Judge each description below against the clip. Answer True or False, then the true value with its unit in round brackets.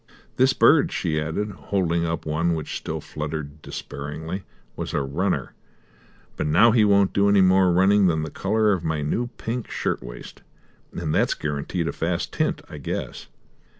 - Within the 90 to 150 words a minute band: False (170 wpm)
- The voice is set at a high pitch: False (85 Hz)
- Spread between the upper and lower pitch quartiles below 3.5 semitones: False (4.6 semitones)